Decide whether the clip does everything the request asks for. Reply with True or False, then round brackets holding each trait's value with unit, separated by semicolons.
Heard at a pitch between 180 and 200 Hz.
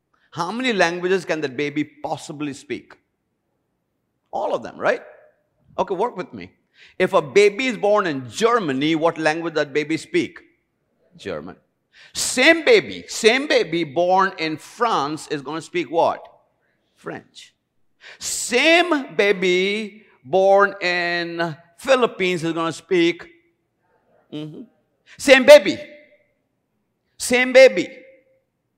True (190 Hz)